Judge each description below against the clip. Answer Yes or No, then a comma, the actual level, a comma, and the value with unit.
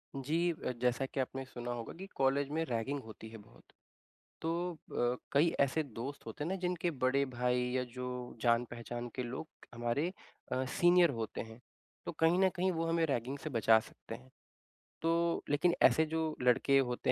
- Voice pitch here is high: No, low, 135 Hz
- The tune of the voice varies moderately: Yes, average, 5.0 semitones